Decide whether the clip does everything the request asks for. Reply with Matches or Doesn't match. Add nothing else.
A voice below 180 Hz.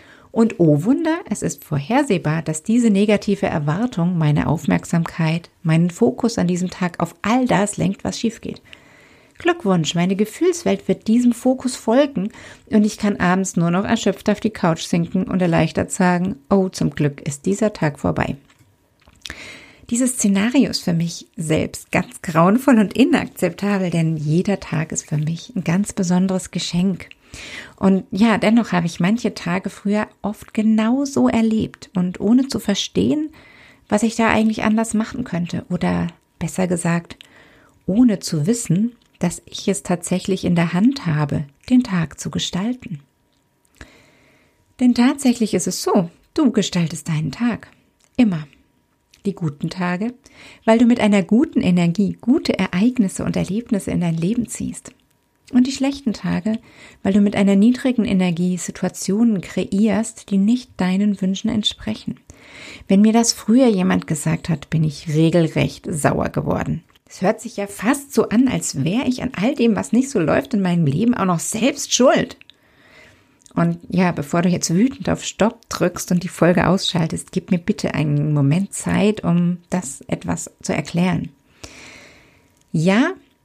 Doesn't match